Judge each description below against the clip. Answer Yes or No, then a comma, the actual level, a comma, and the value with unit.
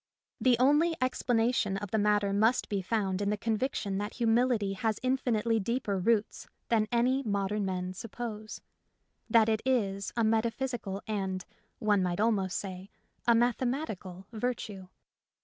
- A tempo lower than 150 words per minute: Yes, average, 140 wpm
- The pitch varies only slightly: No, average, 3.3 semitones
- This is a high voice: Yes, high, 215 Hz